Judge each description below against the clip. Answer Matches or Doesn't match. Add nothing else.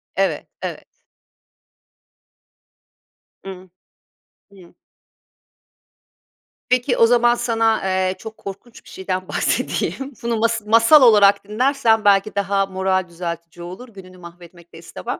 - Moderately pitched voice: Doesn't match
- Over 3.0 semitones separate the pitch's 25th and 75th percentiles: Matches